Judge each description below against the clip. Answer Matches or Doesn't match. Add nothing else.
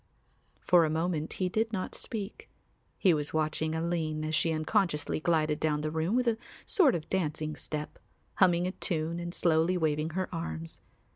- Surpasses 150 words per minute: Matches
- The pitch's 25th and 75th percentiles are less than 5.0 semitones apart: Matches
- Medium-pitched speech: Matches